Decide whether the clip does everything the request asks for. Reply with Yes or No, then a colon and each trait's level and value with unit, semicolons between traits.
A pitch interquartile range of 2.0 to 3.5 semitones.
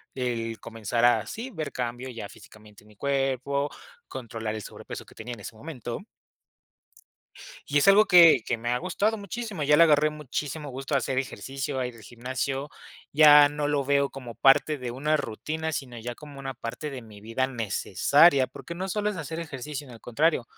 No: average, 4.1 semitones